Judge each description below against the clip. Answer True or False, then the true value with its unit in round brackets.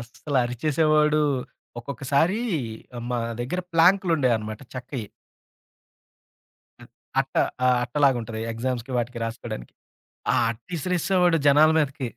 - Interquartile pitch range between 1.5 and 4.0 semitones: False (4.6 semitones)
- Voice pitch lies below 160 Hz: True (135 Hz)